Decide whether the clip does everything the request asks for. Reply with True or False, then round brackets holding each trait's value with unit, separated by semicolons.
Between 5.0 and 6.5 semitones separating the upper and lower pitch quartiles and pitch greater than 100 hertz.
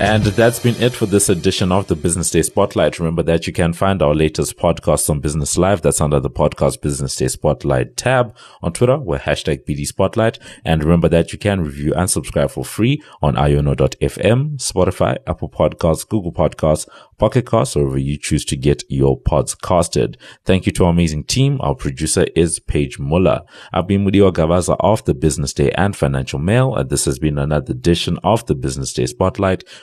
False (5.5 semitones; 85 Hz)